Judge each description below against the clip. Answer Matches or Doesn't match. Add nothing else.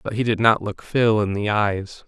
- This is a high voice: Doesn't match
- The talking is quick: Matches